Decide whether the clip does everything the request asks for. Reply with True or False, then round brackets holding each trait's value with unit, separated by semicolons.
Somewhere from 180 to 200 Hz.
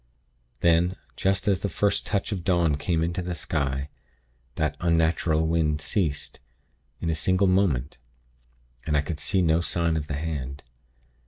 False (80 Hz)